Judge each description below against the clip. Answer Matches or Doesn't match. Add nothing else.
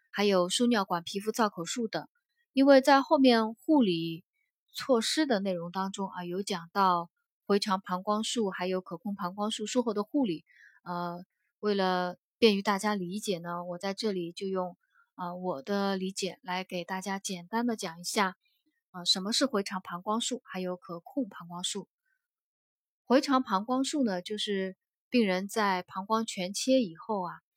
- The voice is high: Matches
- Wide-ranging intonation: Doesn't match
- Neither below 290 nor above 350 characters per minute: Doesn't match